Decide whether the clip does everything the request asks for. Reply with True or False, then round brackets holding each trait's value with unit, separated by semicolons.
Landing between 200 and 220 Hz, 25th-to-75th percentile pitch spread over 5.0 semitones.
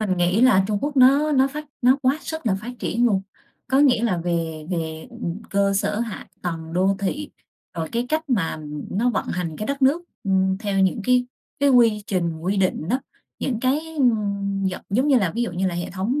True (210 Hz; 5.4 semitones)